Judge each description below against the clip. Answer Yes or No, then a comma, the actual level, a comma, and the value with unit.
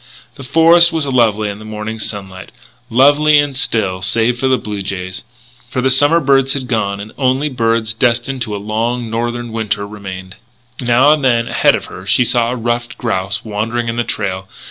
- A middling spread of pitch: Yes, average, 3.7 semitones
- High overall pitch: No, low, 115 Hz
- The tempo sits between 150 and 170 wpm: No, average, 190 wpm